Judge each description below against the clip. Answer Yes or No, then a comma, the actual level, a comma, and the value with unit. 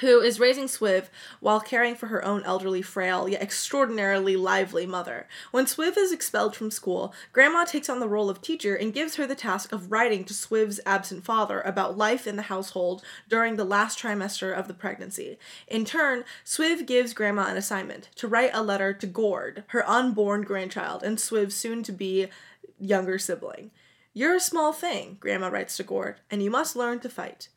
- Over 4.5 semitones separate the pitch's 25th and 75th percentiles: No, average, 4.0 semitones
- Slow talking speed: No, average, 190 wpm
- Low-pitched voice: No, high, 215 Hz